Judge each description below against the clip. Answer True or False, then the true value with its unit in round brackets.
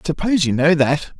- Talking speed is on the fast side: True (250 wpm)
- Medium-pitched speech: True (160 Hz)